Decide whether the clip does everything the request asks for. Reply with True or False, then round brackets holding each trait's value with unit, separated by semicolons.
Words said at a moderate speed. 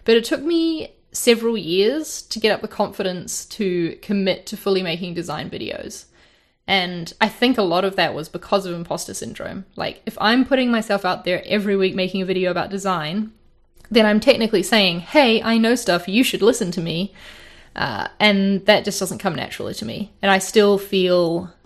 True (195 wpm)